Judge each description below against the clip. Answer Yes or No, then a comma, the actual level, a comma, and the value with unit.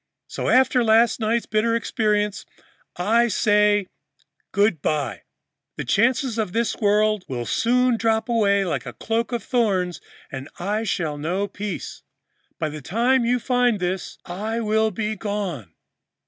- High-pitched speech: Yes, high, 215 Hz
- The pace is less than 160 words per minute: Yes, average, 145 wpm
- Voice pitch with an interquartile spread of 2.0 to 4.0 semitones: Yes, average, 3.6 semitones